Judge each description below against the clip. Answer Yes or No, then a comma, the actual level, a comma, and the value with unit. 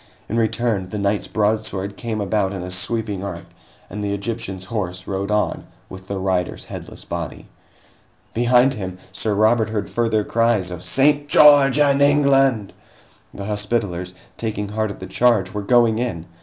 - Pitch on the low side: Yes, low, 105 Hz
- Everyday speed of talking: Yes, average, 160 wpm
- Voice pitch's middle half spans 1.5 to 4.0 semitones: Yes, average, 3.4 semitones